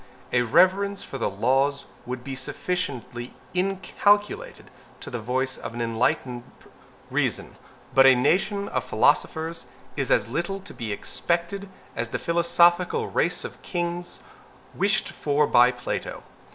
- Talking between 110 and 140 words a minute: Yes, slow, 135 wpm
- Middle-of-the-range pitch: Yes, medium, 155 Hz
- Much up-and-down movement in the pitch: Yes, wide, 6.4 semitones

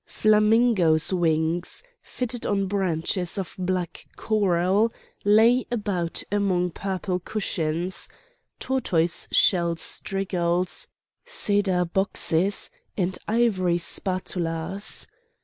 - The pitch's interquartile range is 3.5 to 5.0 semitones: No, average, 3.0 semitones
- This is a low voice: No, medium, 185 Hz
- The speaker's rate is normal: No, slow, 80 wpm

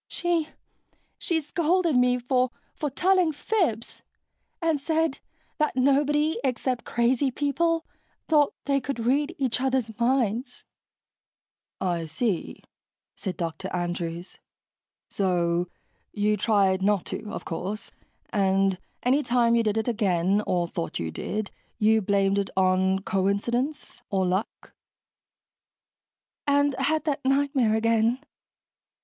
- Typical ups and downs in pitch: No, wide, 6.5 semitones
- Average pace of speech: No, slow, 115 wpm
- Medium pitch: No, high, 235 Hz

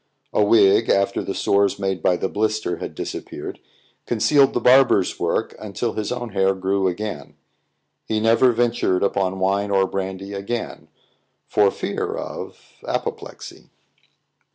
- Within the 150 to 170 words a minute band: No, slow, 135 wpm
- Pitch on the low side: Yes, low, 100 Hz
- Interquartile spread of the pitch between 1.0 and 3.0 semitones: Yes, average, 2.7 semitones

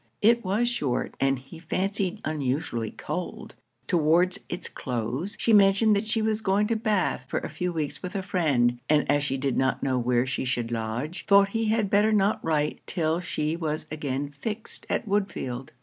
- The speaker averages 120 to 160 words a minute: No, average, 185 wpm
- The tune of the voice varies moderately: No, wide, 7.0 semitones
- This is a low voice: No, medium, 165 Hz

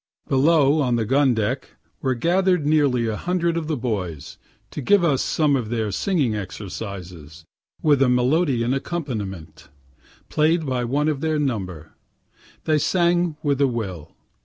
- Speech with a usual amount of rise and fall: No, wide, 6.2 semitones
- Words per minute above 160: No, average, 150 wpm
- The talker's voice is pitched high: No, low, 130 Hz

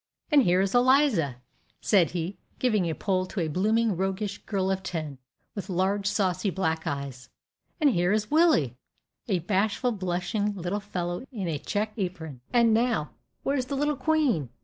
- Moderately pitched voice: No, high, 195 Hz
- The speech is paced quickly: No, average, 165 wpm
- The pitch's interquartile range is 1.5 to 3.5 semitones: No, average, 4.3 semitones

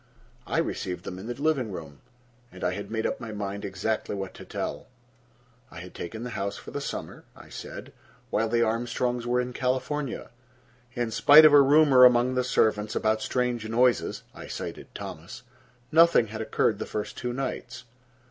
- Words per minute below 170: No, average, 175 wpm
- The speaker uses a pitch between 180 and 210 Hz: No, low, 120 Hz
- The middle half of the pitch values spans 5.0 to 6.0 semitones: No, average, 3.2 semitones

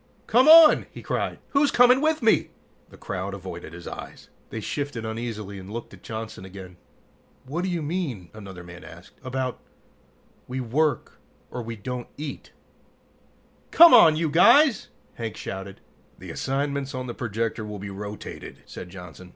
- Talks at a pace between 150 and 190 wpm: Yes, average, 160 wpm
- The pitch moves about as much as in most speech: No, wide, 7.8 semitones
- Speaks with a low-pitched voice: Yes, low, 115 Hz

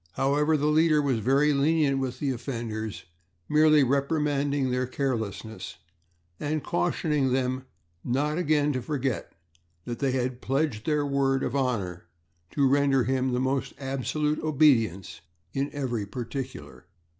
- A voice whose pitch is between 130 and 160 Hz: Yes, low, 135 Hz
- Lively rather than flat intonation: No, average, 2.7 semitones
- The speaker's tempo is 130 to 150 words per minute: Yes, slow, 135 wpm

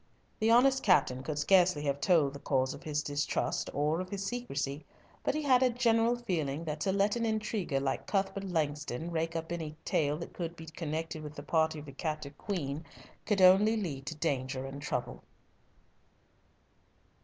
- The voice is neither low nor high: Yes, medium, 160 Hz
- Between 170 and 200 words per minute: Yes, average, 180 wpm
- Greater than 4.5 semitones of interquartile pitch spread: Yes, average, 5.1 semitones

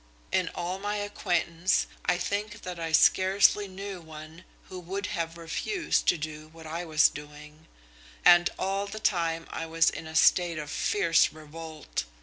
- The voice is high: No, medium, 170 Hz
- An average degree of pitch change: Yes, average, 3.1 semitones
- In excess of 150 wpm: Yes, average, 160 wpm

